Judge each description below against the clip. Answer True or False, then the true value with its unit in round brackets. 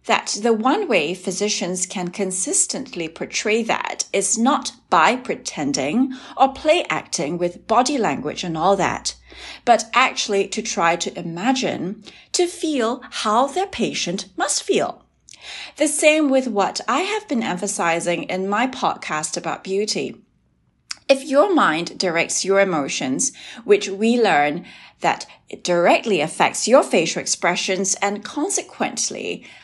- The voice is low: False (205 Hz)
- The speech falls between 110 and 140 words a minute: True (135 wpm)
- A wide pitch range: True (6.4 semitones)